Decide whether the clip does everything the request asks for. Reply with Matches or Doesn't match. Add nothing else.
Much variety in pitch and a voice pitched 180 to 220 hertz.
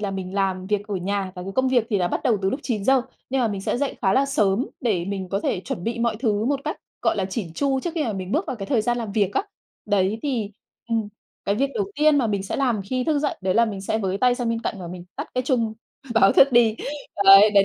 Doesn't match